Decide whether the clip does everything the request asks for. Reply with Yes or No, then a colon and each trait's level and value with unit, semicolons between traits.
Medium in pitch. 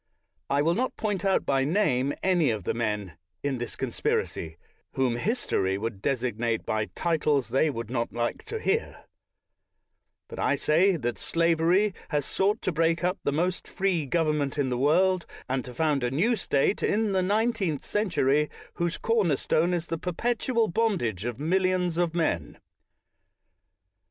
Yes: medium, 160 Hz